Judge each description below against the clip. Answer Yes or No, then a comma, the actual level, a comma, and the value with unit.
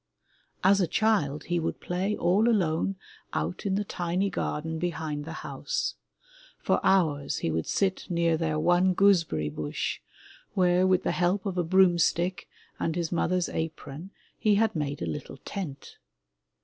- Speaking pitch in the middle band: Yes, medium, 175 Hz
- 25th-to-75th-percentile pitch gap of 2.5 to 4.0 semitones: Yes, average, 3.3 semitones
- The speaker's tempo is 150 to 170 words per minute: Yes, average, 160 wpm